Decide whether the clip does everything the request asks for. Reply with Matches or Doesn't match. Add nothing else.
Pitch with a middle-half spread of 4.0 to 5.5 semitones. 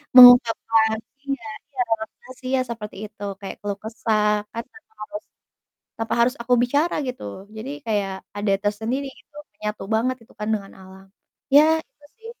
Doesn't match